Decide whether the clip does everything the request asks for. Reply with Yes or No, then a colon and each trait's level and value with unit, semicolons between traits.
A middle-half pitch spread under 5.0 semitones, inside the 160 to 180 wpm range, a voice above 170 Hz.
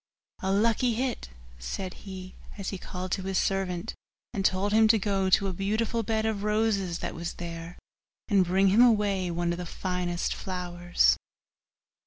Yes: average, 2.9 semitones; average, 170 wpm; high, 190 Hz